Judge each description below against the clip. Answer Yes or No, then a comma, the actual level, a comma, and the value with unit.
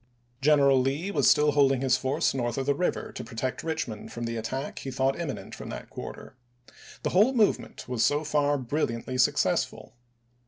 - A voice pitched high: No, low, 135 Hz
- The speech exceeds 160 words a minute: Yes, average, 180 wpm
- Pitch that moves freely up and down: No, average, 2.7 semitones